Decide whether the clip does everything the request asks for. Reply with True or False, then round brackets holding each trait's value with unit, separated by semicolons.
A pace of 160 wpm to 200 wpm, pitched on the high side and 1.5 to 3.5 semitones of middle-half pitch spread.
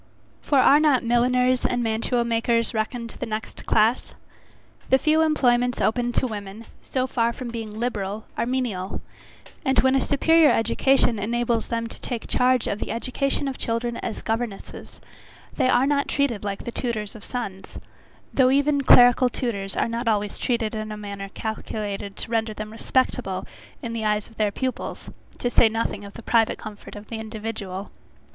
True (170 wpm; 230 Hz; 2.7 semitones)